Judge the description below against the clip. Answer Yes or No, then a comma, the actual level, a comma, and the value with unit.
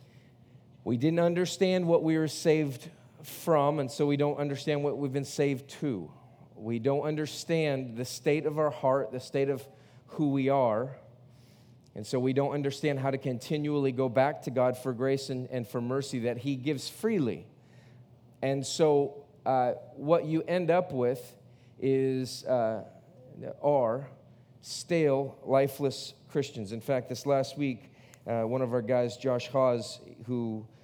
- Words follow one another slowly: No, average, 160 wpm